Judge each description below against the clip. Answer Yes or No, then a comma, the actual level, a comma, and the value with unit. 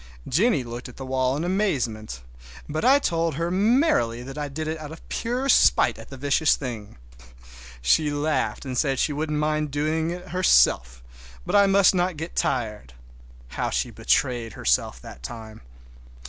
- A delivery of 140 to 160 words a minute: No, average, 170 wpm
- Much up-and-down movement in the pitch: Yes, wide, 5.7 semitones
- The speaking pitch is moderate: Yes, medium, 145 Hz